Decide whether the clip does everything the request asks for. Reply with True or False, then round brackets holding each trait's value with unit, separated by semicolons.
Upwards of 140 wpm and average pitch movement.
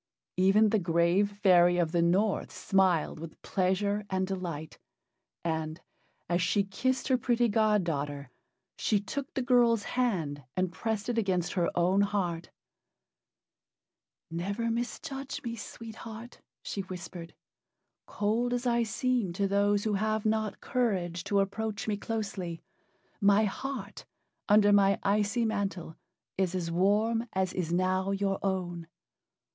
False (135 wpm; 3.8 semitones)